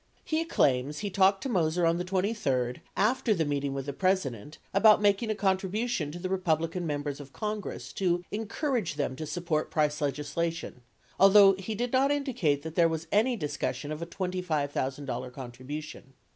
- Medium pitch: Yes, medium, 170 Hz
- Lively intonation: Yes, wide, 5.7 semitones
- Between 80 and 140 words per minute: No, average, 170 wpm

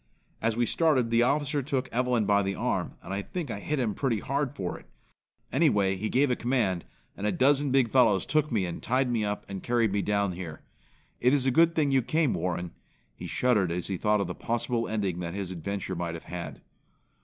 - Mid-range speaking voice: No, low, 115 Hz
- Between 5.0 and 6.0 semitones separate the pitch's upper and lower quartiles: Yes, wide, 5.4 semitones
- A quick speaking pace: Yes, fast, 225 wpm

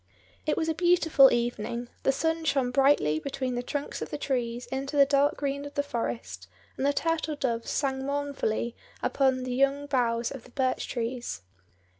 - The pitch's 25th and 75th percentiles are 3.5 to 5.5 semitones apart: No, average, 2.9 semitones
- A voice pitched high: Yes, very high, 270 Hz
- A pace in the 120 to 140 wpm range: No, average, 180 wpm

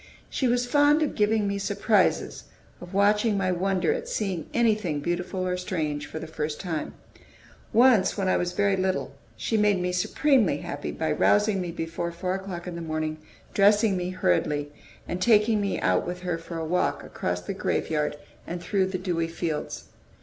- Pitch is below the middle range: No, medium, 185 Hz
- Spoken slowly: No, average, 180 wpm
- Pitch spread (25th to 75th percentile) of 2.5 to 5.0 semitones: Yes, average, 3.8 semitones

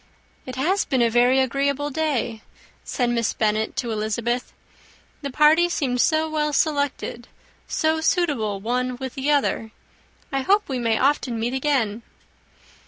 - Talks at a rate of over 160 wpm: No, average, 145 wpm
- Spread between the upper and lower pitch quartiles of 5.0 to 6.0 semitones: No, average, 4.0 semitones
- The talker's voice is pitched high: Yes, very high, 260 Hz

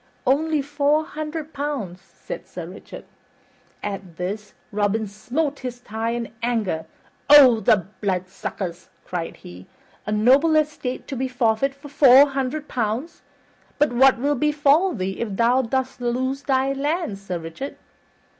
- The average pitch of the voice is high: Yes, very high, 250 Hz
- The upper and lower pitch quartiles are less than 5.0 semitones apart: No, wide, 5.6 semitones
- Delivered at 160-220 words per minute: No, average, 140 wpm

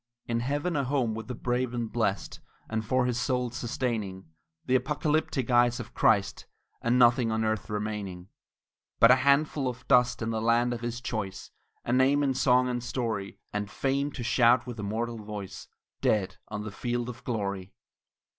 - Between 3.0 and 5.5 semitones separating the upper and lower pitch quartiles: No, narrow, 2.5 semitones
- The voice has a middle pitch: No, low, 120 Hz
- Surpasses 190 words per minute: No, average, 175 wpm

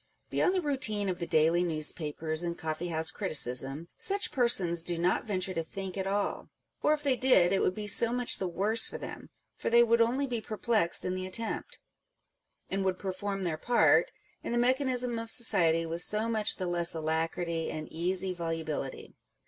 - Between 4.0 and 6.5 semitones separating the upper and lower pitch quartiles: Yes, wide, 5.5 semitones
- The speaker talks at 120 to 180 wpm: No, average, 190 wpm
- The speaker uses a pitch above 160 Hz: Yes, medium, 185 Hz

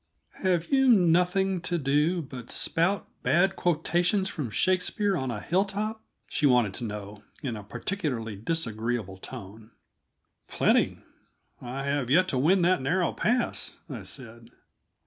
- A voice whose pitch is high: No, medium, 155 Hz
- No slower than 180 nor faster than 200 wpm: No, slow, 135 wpm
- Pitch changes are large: Yes, wide, 7.9 semitones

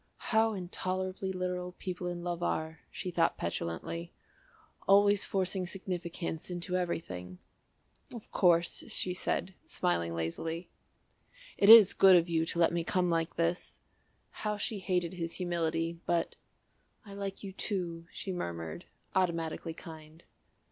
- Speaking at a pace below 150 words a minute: Yes, slow, 135 wpm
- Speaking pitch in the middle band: Yes, medium, 175 Hz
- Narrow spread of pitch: Yes, narrow, 2.1 semitones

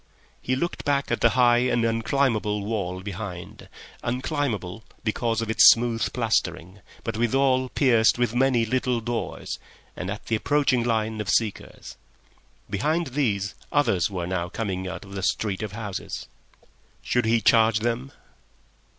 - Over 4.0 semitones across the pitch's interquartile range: No, average, 3.5 semitones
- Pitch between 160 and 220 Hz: No, low, 115 Hz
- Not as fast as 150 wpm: Yes, average, 140 wpm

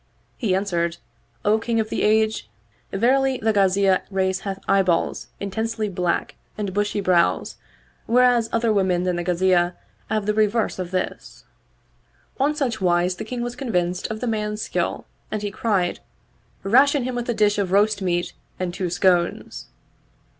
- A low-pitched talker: No, high, 200 Hz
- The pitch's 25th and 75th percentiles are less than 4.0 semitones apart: Yes, average, 3.3 semitones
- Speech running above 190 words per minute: No, average, 165 wpm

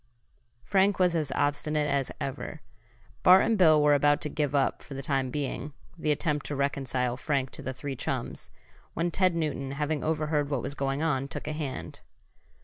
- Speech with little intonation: Yes, narrow, 2.2 semitones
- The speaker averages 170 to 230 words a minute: Yes, average, 185 wpm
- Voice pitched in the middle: Yes, medium, 145 Hz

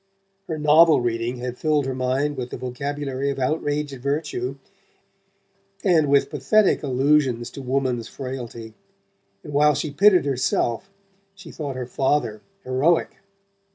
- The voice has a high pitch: No, medium, 140 Hz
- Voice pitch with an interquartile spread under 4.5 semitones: Yes, average, 2.9 semitones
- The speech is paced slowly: Yes, slow, 130 wpm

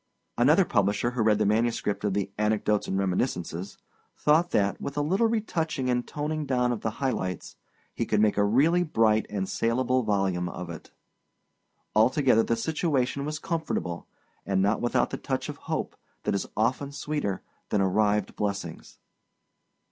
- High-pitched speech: No, low, 110 Hz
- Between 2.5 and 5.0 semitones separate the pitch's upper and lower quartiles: No, wide, 5.6 semitones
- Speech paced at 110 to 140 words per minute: No, average, 165 wpm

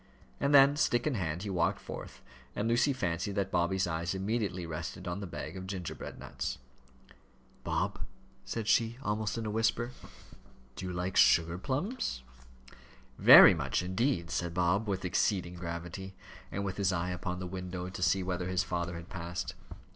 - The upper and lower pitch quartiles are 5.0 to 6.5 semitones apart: No, average, 3.2 semitones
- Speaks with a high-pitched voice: No, very low, 95 Hz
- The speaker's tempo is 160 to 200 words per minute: Yes, average, 170 wpm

